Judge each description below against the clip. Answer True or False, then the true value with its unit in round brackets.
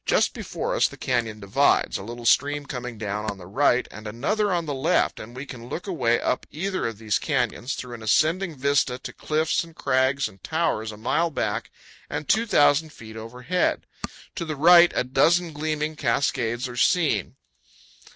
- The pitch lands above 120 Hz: True (135 Hz)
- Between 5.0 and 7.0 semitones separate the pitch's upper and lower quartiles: True (5.3 semitones)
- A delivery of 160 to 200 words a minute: True (180 wpm)